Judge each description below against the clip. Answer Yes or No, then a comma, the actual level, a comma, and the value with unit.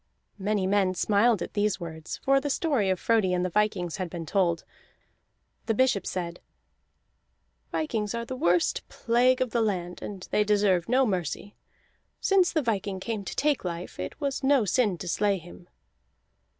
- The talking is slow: No, average, 170 wpm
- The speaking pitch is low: No, high, 205 Hz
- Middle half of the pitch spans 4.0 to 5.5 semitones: Yes, average, 4.6 semitones